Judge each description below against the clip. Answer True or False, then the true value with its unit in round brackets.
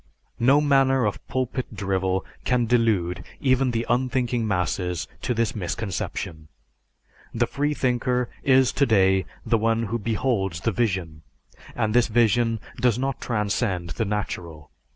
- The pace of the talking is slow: True (130 wpm)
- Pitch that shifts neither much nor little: True (4.5 semitones)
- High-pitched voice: False (115 Hz)